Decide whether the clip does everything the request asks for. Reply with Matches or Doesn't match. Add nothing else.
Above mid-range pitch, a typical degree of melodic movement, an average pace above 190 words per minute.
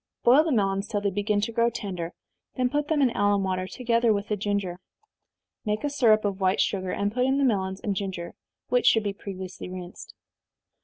Matches